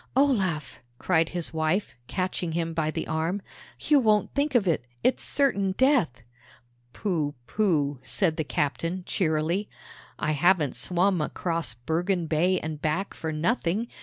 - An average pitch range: Yes, average, 3.9 semitones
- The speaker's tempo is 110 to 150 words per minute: Yes, average, 140 wpm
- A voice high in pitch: No, medium, 170 Hz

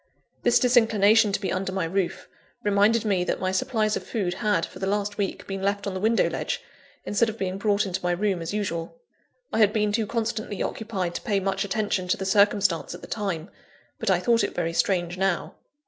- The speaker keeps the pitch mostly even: Yes, narrow, 2.2 semitones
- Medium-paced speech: No, fast, 215 wpm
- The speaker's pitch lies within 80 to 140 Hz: No, high, 200 Hz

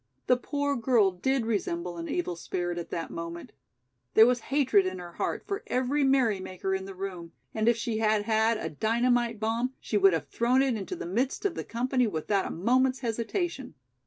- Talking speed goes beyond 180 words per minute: Yes, average, 195 wpm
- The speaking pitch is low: No, high, 225 Hz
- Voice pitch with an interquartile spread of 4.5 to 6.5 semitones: Yes, average, 5.2 semitones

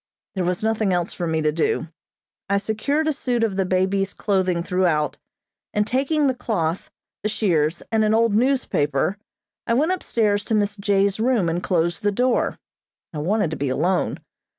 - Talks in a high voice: Yes, high, 200 Hz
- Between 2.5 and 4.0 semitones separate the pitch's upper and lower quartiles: No, average, 4.4 semitones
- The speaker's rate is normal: Yes, average, 175 wpm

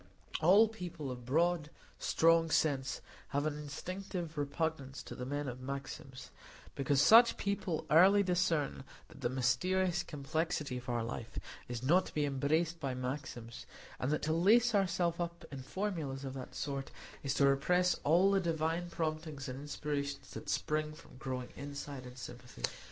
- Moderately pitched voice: Yes, medium, 150 Hz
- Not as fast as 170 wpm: Yes, average, 160 wpm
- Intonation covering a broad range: No, average, 4.2 semitones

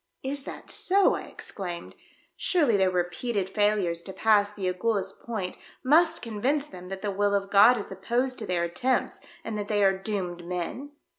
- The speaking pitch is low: No, high, 205 Hz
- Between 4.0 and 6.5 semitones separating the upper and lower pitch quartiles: Yes, average, 4.3 semitones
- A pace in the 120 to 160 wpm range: No, average, 175 wpm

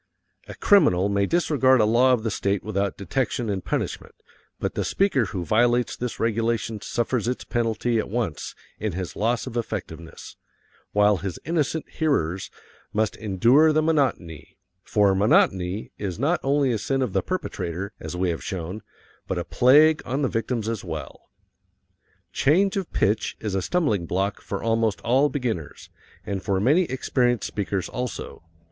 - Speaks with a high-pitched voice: No, low, 115 Hz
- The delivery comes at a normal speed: Yes, average, 160 wpm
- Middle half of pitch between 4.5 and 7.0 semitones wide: Yes, average, 4.9 semitones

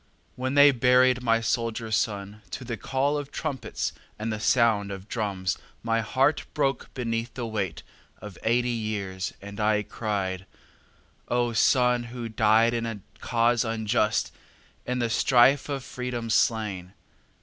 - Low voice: Yes, low, 115 Hz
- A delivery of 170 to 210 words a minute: No, average, 145 wpm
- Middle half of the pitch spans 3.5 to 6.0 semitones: No, average, 2.7 semitones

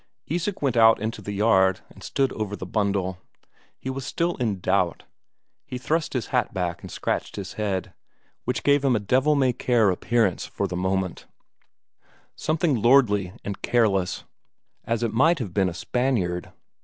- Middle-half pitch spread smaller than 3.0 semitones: No, average, 5.3 semitones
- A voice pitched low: Yes, low, 110 Hz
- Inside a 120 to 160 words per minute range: No, average, 170 wpm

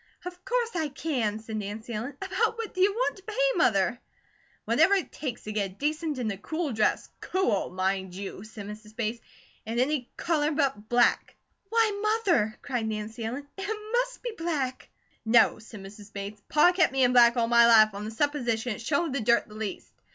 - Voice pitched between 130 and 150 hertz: No, high, 245 Hz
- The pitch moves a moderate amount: No, wide, 7.5 semitones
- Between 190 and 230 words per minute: Yes, average, 200 wpm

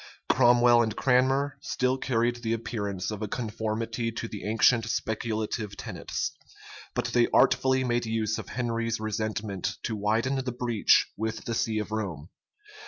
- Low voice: Yes, low, 115 Hz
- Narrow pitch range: Yes, narrow, 2.0 semitones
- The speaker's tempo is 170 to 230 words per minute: No, average, 150 wpm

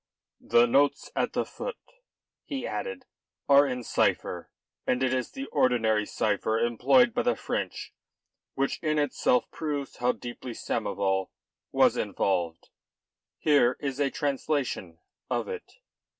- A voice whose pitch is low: Yes, low, 130 Hz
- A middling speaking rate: No, slow, 130 wpm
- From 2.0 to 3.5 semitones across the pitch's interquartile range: No, average, 4.3 semitones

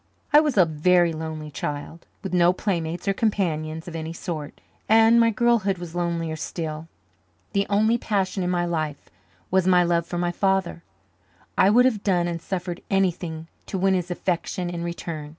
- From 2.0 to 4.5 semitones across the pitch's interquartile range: Yes, average, 2.9 semitones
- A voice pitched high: No, medium, 175 Hz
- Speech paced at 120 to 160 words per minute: No, average, 175 wpm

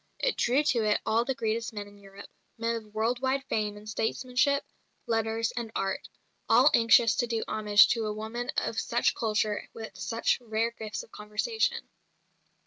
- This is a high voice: Yes, high, 225 Hz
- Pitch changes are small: Yes, narrow, 2.0 semitones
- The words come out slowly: No, average, 180 wpm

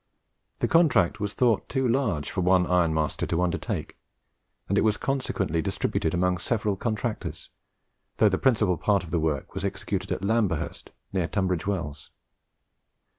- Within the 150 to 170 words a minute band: Yes, average, 155 wpm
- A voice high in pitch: No, very low, 95 Hz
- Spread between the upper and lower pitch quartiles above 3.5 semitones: Yes, average, 4.3 semitones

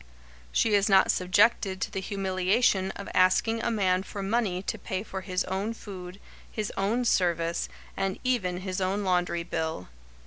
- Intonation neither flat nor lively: No, narrow, 2.0 semitones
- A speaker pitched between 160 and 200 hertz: Yes, high, 190 Hz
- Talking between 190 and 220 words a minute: No, average, 165 wpm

